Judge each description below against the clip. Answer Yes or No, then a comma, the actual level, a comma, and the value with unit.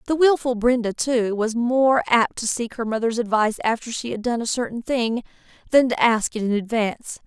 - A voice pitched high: Yes, high, 235 Hz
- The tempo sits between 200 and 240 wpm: Yes, fast, 205 wpm